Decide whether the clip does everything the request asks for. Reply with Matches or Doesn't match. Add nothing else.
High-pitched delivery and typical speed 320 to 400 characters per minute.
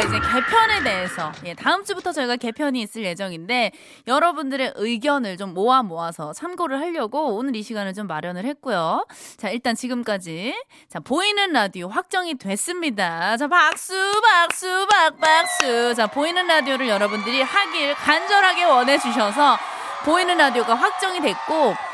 Matches